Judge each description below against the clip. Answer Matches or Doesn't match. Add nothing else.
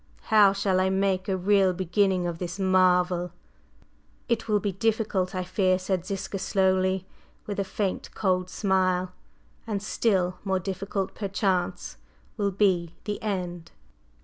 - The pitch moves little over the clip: Matches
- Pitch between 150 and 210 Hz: Matches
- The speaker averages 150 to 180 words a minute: Doesn't match